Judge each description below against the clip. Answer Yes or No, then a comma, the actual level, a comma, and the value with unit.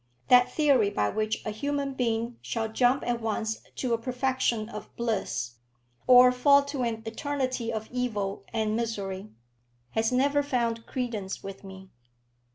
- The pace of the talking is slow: No, average, 150 wpm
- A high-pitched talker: Yes, high, 230 Hz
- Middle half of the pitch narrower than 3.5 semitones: Yes, average, 2.8 semitones